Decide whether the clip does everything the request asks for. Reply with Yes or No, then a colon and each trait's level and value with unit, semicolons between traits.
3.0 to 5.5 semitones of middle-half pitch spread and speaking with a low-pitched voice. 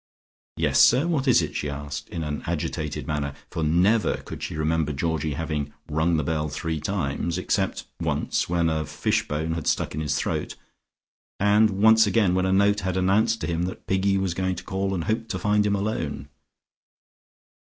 Yes: average, 4.5 semitones; very low, 85 Hz